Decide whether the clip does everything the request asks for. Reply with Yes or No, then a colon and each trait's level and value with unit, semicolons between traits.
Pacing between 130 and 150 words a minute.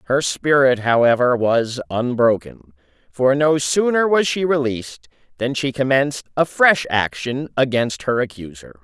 Yes: slow, 135 wpm